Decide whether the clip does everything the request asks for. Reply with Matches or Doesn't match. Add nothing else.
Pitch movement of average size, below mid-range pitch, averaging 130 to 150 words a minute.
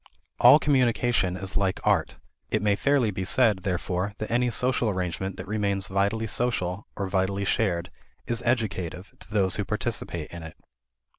Doesn't match